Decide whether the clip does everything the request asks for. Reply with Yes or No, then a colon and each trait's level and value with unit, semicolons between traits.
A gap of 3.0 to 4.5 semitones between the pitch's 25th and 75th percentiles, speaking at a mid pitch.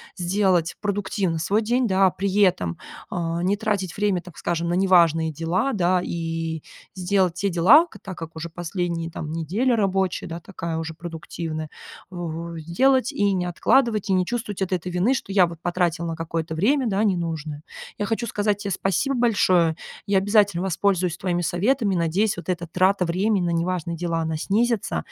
Yes: average, 3.3 semitones; medium, 180 Hz